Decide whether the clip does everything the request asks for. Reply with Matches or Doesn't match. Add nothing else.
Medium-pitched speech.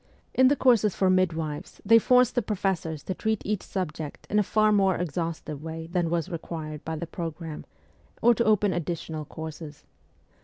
Matches